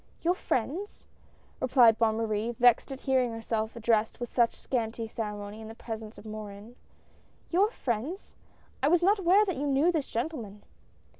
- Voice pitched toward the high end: Yes, high, 235 Hz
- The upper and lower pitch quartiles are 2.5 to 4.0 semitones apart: No, average, 4.8 semitones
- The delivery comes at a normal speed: Yes, average, 160 wpm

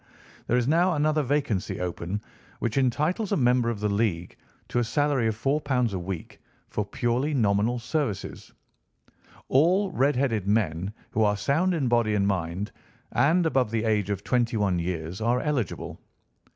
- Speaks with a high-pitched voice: No, low, 115 Hz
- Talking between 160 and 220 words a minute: Yes, average, 165 wpm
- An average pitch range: No, wide, 5.7 semitones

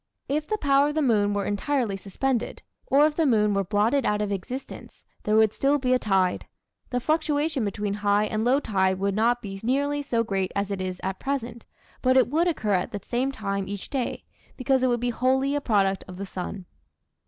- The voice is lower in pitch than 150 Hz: No, high, 230 Hz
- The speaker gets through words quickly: Yes, fast, 215 wpm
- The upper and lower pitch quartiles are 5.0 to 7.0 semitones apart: Yes, average, 5.3 semitones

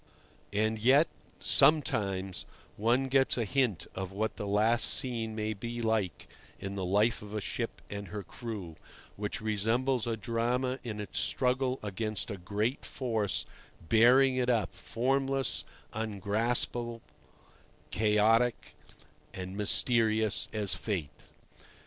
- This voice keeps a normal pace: No, slow, 125 wpm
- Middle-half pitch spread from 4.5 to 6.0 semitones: No, average, 3.0 semitones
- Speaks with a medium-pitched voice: No, low, 110 Hz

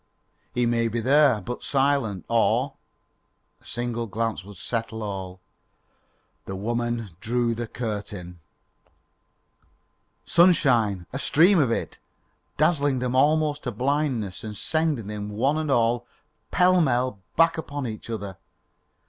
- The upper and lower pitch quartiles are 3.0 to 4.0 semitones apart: No, average, 5.1 semitones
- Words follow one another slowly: Yes, slow, 125 wpm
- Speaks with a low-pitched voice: Yes, low, 120 Hz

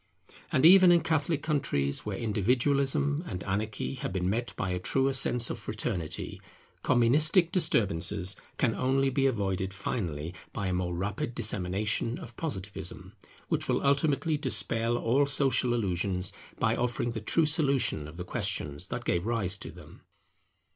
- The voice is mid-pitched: No, low, 115 Hz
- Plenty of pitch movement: Yes, wide, 6.4 semitones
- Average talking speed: Yes, average, 150 wpm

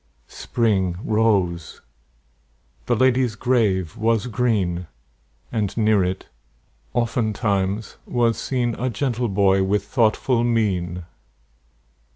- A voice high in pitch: No, low, 110 Hz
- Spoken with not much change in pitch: No, average, 3.7 semitones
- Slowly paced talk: Yes, slow, 95 wpm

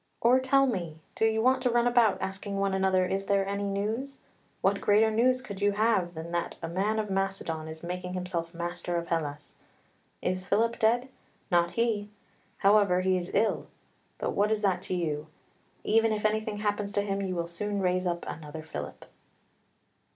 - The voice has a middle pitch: No, high, 195 Hz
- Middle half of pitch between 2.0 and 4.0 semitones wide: Yes, average, 3.6 semitones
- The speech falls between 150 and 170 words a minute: No, average, 185 wpm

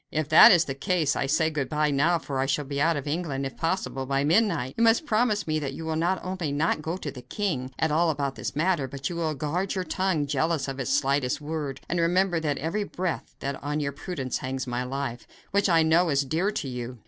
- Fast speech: Yes, fast, 250 wpm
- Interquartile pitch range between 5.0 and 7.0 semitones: No, average, 3.9 semitones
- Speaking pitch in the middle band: Yes, medium, 155 Hz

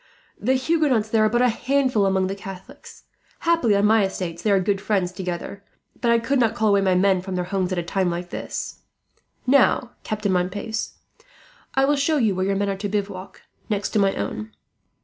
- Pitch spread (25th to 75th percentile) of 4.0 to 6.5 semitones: No, average, 3.6 semitones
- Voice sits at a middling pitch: No, high, 200 Hz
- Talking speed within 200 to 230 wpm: Yes, fast, 205 wpm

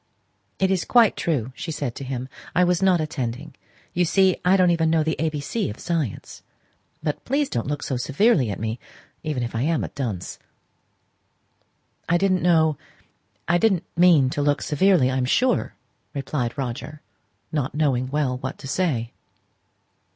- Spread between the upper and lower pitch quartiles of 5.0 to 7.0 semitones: Yes, wide, 5.4 semitones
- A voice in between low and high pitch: Yes, medium, 150 Hz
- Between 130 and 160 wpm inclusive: No, average, 175 wpm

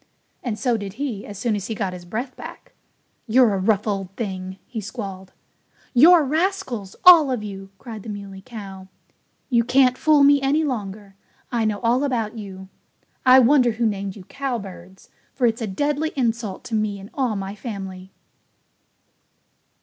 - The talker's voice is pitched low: No, high, 220 Hz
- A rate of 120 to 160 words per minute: No, average, 170 wpm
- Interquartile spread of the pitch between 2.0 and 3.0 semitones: No, average, 4.6 semitones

